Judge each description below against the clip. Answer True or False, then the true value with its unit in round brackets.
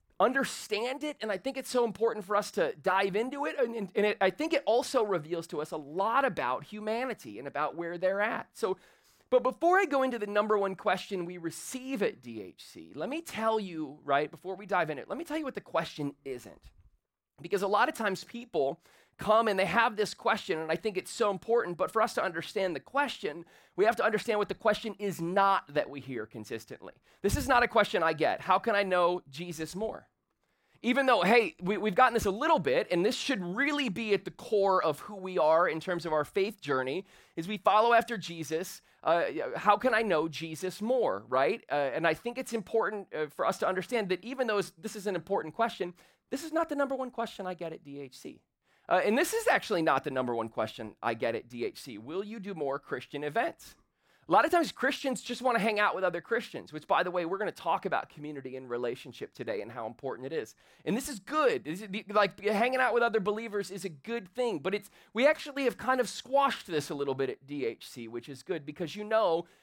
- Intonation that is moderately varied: False (6.2 semitones)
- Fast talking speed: True (240 wpm)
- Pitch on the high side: True (205 Hz)